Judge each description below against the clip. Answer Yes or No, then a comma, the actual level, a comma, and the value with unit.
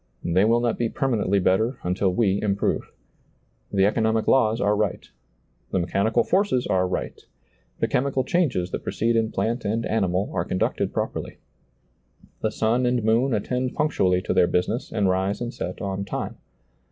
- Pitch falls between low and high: No, low, 110 Hz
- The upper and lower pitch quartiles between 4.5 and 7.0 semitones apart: No, average, 3.9 semitones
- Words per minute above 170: No, average, 165 wpm